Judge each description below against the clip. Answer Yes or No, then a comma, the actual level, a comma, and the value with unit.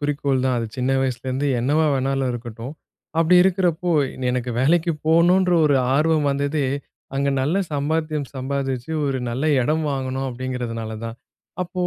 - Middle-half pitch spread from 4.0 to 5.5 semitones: No, average, 3.4 semitones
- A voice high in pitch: No, medium, 140 Hz